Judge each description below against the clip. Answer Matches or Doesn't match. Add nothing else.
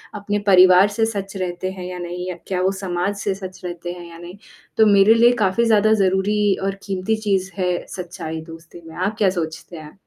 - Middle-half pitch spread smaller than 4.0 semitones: Matches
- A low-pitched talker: Doesn't match